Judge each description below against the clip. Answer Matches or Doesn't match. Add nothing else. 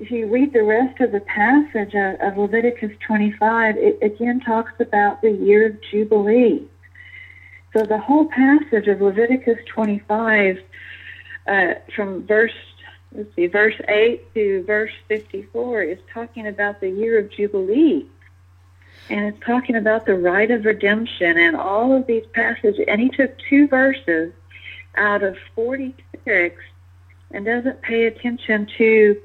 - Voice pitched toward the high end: Matches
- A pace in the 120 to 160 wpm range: Matches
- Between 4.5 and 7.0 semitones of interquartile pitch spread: Doesn't match